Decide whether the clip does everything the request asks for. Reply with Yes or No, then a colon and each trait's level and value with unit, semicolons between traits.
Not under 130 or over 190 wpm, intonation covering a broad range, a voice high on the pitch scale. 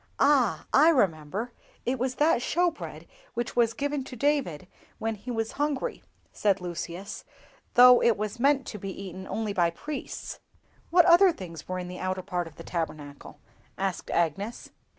Yes: average, 170 wpm; wide, 6.6 semitones; high, 220 Hz